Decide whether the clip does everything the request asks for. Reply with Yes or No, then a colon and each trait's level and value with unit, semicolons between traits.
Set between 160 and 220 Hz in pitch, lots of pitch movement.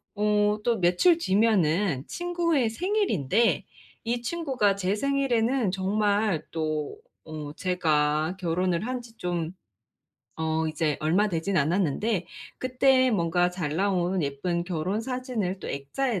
Yes: high, 190 Hz; wide, 6.1 semitones